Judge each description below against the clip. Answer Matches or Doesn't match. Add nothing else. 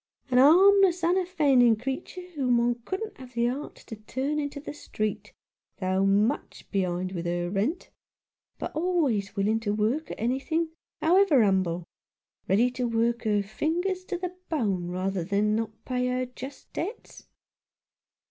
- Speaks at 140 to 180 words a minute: Matches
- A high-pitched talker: Matches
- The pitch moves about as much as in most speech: Doesn't match